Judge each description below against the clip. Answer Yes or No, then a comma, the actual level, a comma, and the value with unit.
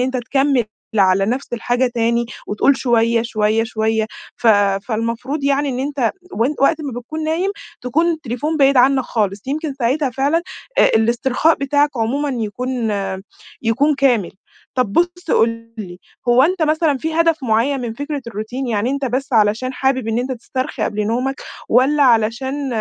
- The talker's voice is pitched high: Yes, very high, 255 Hz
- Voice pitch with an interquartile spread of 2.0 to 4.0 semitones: Yes, average, 3.6 semitones